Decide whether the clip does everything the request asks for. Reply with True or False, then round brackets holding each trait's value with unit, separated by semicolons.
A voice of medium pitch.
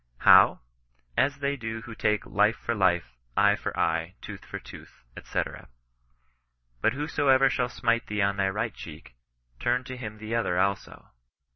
False (105 Hz)